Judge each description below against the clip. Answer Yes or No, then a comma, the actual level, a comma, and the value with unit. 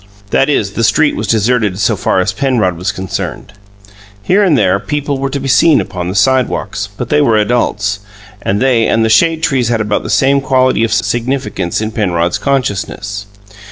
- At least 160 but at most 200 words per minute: Yes, average, 190 wpm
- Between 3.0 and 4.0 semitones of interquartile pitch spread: No, average, 4.7 semitones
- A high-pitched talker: No, low, 115 Hz